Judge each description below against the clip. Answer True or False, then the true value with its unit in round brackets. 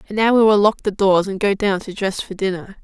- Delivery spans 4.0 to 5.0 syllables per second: False (6.0 syllables/s)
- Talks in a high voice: True (200 Hz)